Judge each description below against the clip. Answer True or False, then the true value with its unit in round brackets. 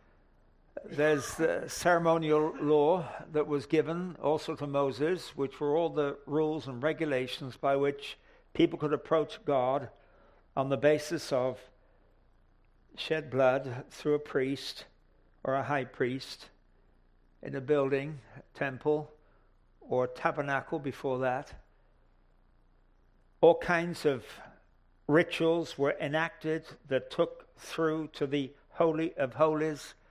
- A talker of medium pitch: True (145 Hz)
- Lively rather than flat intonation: False (3.3 semitones)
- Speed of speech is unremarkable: False (120 wpm)